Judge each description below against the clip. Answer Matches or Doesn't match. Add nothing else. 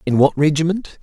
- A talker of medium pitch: Matches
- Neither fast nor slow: Matches